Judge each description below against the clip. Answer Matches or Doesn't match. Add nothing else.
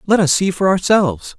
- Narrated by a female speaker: Doesn't match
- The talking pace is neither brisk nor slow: Doesn't match